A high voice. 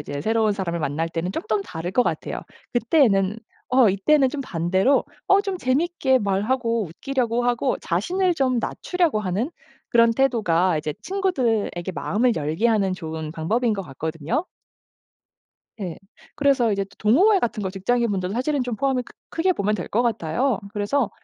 Yes: high, 225 Hz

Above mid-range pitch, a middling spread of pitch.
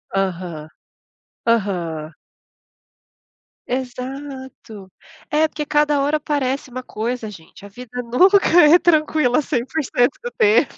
No: very high, 255 Hz; wide, 5.7 semitones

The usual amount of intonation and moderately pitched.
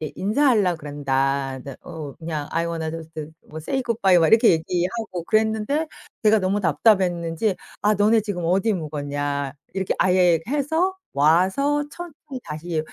No: wide, 5.7 semitones; medium, 180 Hz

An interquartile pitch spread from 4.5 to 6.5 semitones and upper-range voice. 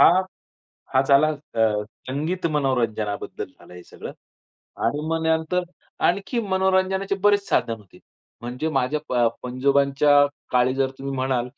No: average, 5.1 semitones; medium, 140 Hz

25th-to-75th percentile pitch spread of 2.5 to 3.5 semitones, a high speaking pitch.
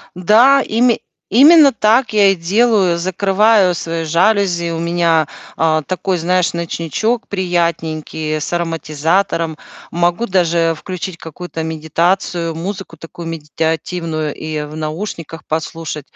No: average, 3.1 semitones; medium, 170 Hz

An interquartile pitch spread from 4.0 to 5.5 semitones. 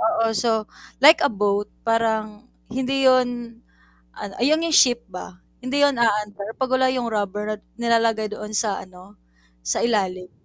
No: average, 3.2 semitones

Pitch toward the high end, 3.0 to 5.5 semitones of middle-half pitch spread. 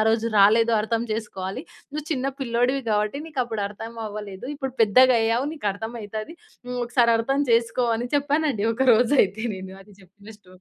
Yes: high, 230 Hz; average, 3.5 semitones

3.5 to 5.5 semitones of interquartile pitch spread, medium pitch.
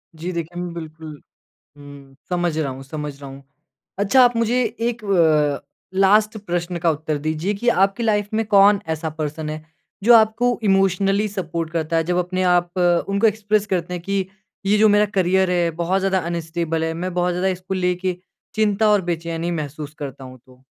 Yes: average, 3.9 semitones; medium, 180 Hz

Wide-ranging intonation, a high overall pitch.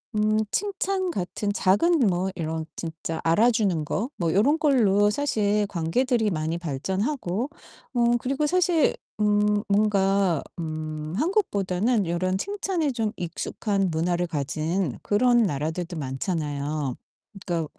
Yes: wide, 6.4 semitones; high, 195 Hz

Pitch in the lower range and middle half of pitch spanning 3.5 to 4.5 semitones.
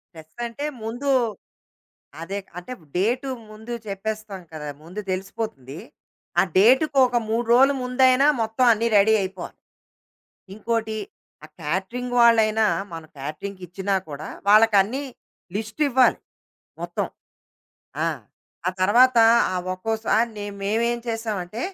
No: high, 220 Hz; average, 3.8 semitones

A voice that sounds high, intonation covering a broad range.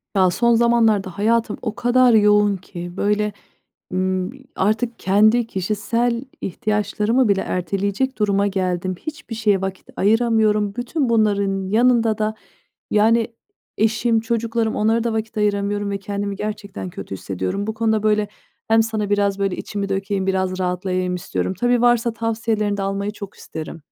No: high, 210 Hz; narrow, 2.6 semitones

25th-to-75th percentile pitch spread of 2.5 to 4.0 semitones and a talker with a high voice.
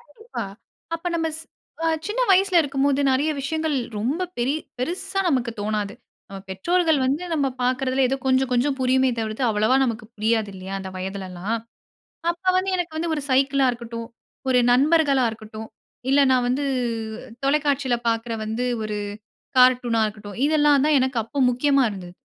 No: average, 4.6 semitones; very high, 260 Hz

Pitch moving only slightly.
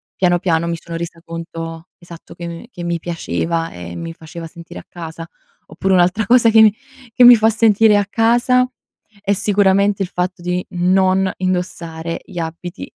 No: average, 3.4 semitones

